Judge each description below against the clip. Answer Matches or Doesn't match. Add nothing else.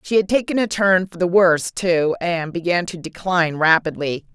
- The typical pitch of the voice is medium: Matches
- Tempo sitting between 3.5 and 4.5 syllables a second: Doesn't match